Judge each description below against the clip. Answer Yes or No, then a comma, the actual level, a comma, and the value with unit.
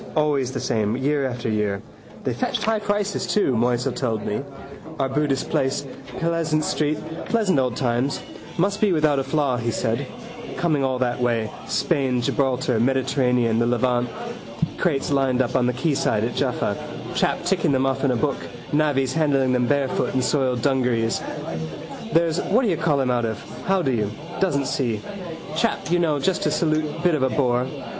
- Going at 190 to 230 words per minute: No, average, 165 wpm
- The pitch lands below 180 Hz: Yes, low, 135 Hz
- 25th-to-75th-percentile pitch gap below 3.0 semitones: No, average, 3.8 semitones